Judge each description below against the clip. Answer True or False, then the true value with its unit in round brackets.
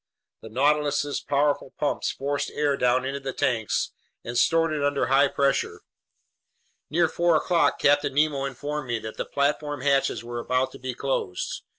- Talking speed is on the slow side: False (165 wpm)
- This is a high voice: False (140 Hz)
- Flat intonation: True (2.2 semitones)